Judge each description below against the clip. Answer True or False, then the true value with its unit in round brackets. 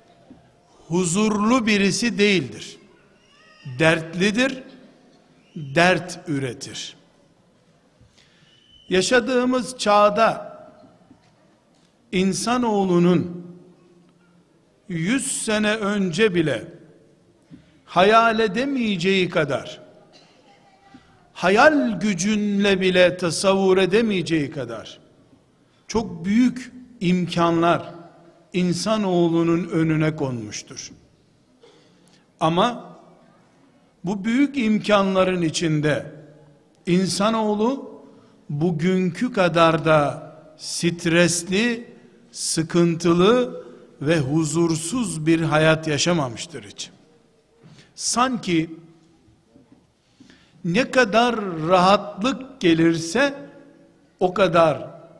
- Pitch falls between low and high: True (180 Hz)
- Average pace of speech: False (60 wpm)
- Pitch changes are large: False (5.0 semitones)